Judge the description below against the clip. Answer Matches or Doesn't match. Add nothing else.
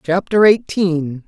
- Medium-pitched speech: Matches